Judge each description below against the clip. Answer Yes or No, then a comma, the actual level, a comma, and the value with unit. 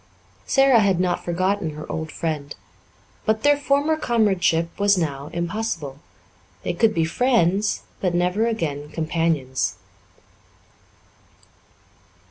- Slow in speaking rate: Yes, slow, 105 wpm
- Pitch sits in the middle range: Yes, medium, 180 Hz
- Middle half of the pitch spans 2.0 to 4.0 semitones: No, wide, 5.4 semitones